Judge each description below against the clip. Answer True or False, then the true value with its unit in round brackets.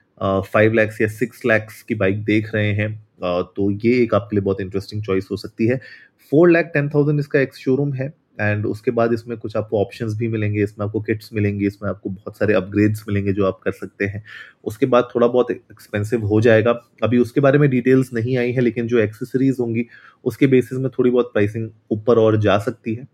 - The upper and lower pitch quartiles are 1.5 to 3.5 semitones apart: True (3.1 semitones)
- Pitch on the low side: True (110 Hz)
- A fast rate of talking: True (220 wpm)